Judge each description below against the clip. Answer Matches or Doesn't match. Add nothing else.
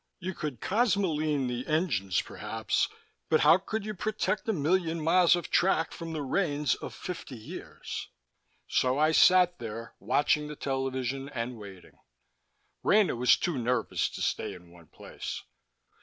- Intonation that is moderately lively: Doesn't match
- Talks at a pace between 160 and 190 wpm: Doesn't match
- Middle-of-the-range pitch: Matches